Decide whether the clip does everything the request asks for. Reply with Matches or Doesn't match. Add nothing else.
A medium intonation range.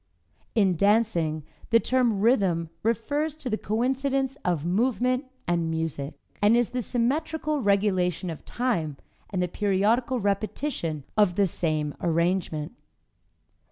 Doesn't match